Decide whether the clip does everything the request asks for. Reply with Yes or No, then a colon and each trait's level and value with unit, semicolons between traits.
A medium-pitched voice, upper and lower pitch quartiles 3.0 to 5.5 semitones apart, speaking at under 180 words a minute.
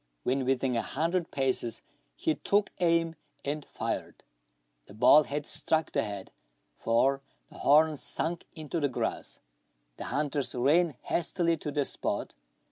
Yes: medium, 150 Hz; average, 3.6 semitones; average, 140 wpm